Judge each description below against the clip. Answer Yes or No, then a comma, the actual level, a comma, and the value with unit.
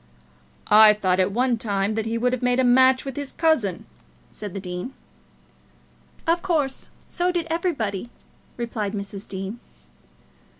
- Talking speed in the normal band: Yes, average, 145 wpm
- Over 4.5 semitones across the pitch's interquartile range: Yes, average, 4.9 semitones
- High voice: Yes, high, 230 Hz